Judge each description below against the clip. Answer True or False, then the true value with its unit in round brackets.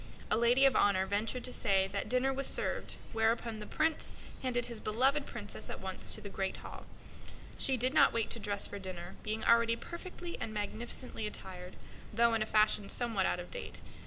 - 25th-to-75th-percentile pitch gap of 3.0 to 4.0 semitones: True (3.5 semitones)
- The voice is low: False (225 Hz)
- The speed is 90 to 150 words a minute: False (195 wpm)